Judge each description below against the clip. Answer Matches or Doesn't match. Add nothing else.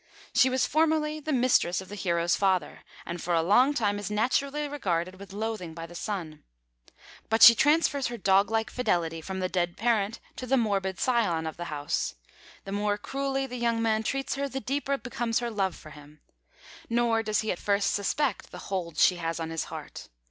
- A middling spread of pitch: Doesn't match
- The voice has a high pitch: Matches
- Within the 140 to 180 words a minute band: Doesn't match